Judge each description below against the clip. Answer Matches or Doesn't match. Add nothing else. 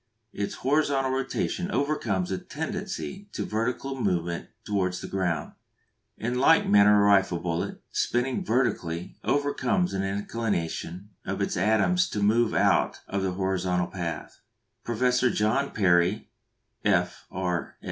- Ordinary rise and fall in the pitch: Doesn't match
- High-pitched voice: Doesn't match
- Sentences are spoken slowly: Matches